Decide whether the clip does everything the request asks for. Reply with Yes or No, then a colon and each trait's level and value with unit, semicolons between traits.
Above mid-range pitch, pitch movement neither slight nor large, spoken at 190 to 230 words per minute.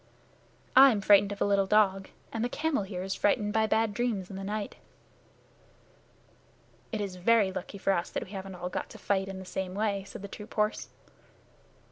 No: high, 200 Hz; narrow, 2.0 semitones; average, 195 wpm